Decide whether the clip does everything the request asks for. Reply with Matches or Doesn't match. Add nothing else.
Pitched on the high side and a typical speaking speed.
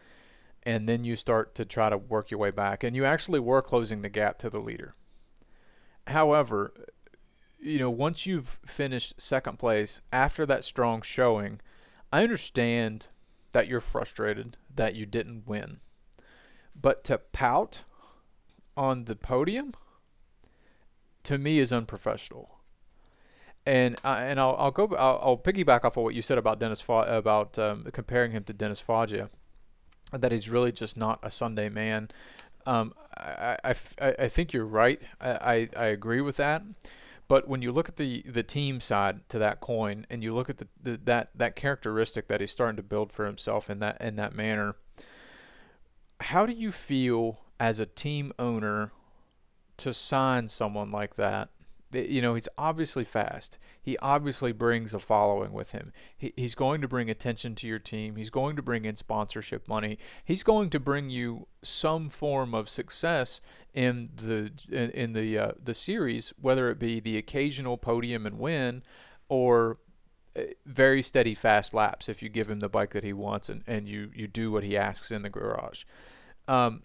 Doesn't match